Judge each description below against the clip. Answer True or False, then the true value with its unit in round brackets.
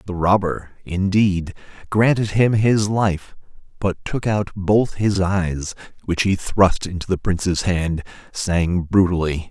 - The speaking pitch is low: True (95 Hz)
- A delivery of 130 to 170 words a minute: True (140 wpm)